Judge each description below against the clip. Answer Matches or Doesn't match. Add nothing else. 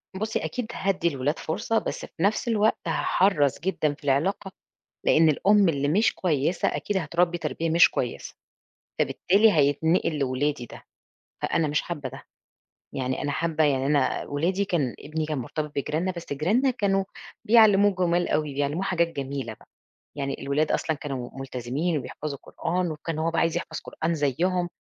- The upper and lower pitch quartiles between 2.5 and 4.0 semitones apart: Doesn't match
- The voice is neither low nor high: Matches